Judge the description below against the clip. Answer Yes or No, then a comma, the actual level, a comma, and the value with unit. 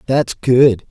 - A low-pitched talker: Yes, low, 125 Hz